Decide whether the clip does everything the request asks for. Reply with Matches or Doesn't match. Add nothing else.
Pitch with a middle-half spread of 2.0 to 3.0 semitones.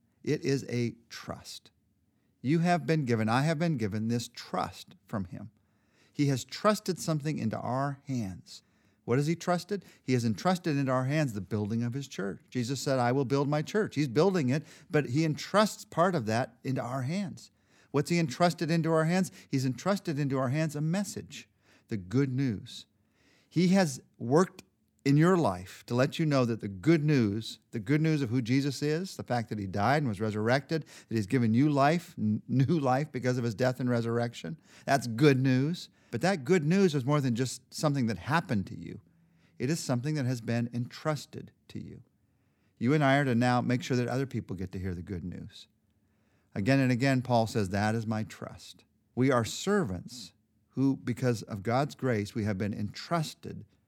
Doesn't match